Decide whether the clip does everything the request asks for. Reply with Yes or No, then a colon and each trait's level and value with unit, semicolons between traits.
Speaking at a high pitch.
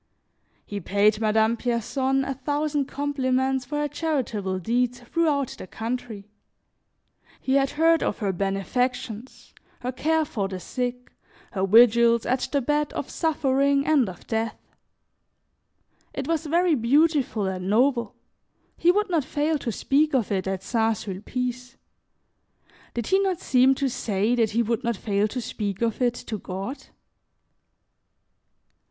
Yes: very high, 250 Hz